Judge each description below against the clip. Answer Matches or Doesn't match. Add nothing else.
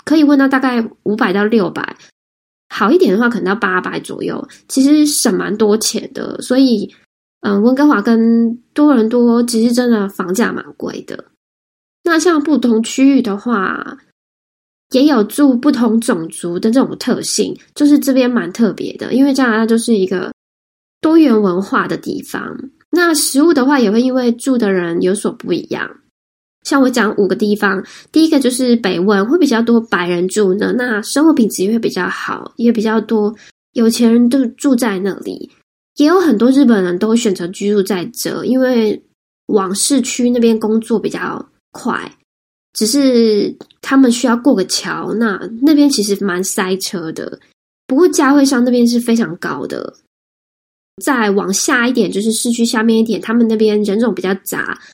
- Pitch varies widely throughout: Doesn't match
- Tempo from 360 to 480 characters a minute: Doesn't match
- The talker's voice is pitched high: Matches